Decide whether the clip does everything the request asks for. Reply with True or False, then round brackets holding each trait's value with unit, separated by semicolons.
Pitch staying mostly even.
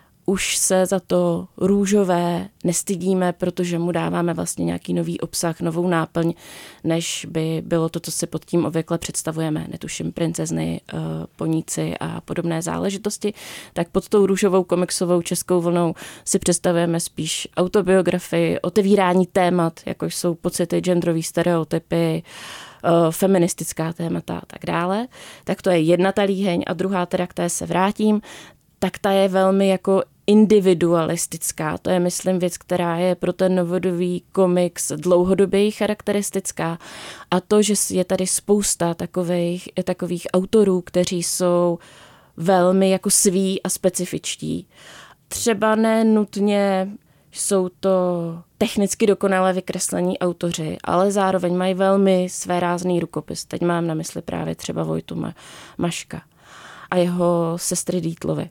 True (2.1 semitones)